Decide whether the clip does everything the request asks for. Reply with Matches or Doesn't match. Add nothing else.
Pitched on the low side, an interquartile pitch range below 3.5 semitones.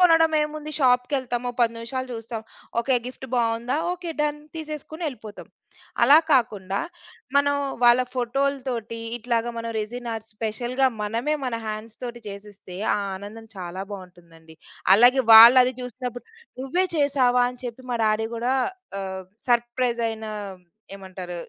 Doesn't match